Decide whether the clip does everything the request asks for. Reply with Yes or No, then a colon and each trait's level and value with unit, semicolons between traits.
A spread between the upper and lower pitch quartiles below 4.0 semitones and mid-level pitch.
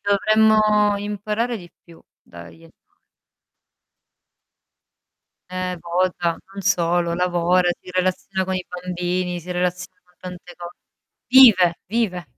Yes: narrow, 2.4 semitones; medium, 180 Hz